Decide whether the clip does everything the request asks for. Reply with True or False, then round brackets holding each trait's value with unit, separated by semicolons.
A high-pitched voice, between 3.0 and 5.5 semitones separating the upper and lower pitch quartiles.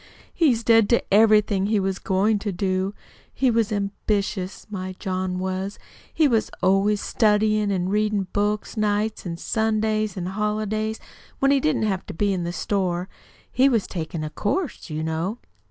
False (205 Hz; 2.5 semitones)